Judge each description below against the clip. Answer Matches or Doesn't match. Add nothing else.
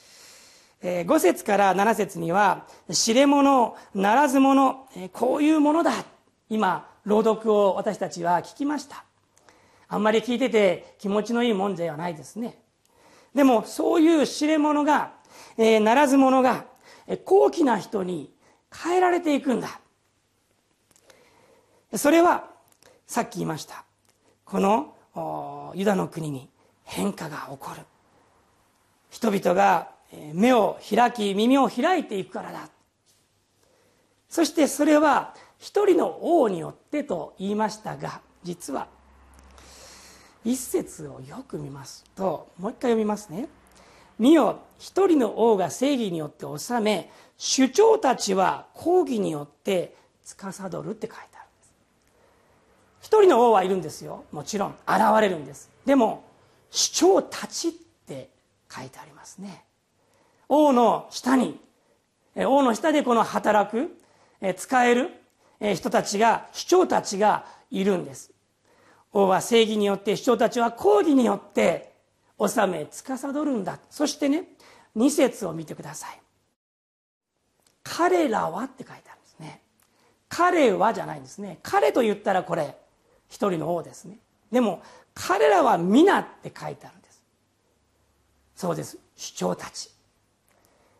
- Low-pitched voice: Doesn't match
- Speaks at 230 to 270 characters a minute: Matches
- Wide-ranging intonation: Matches